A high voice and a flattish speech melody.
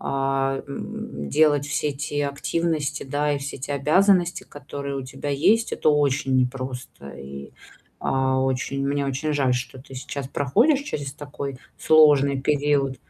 No: medium, 140 Hz; narrow, 1.8 semitones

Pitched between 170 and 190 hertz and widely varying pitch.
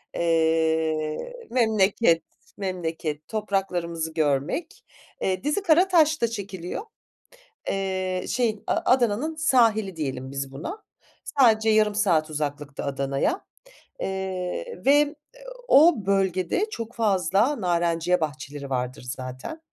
Yes: medium, 185 Hz; wide, 6.5 semitones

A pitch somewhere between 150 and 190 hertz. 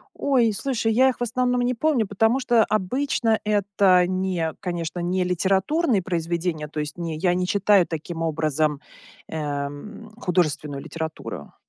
Yes: medium, 185 Hz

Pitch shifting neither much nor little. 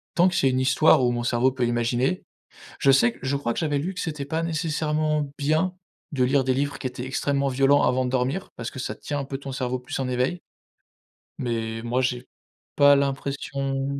No: narrow, 2.3 semitones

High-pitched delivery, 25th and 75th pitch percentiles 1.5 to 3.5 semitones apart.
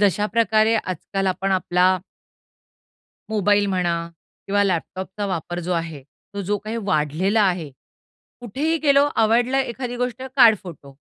No: high, 200 Hz; average, 3.9 semitones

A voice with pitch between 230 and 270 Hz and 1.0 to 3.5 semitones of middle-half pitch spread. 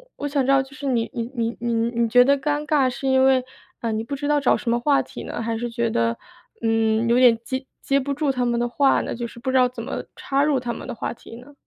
Yes: very high, 250 Hz; average, 2.8 semitones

